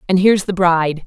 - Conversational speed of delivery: No, fast, 225 wpm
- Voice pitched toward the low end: No, medium, 180 Hz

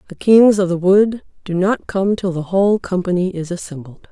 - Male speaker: No, female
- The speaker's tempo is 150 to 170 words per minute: No, fast, 205 wpm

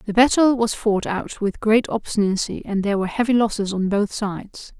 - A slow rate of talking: No, average, 200 wpm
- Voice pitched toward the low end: No, high, 210 Hz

